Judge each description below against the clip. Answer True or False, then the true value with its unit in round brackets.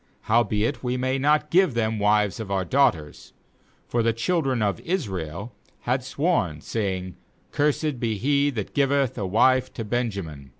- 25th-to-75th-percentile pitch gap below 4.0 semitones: False (5.3 semitones)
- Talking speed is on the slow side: False (155 wpm)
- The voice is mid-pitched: False (115 Hz)